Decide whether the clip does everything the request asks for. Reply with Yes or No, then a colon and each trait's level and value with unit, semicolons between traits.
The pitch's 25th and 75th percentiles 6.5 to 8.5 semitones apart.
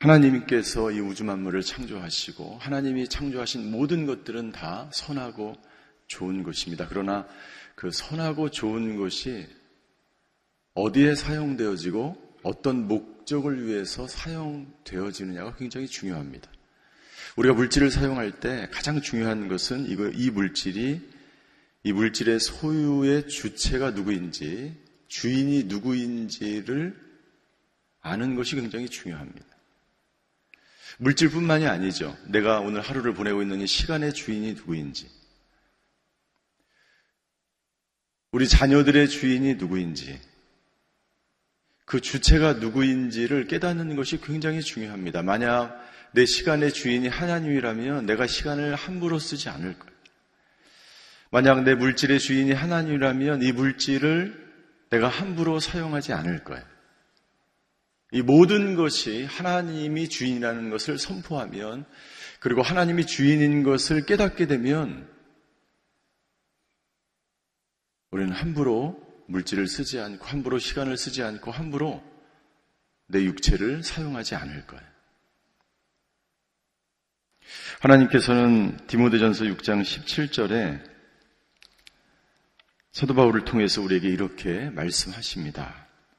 No: wide, 5.6 semitones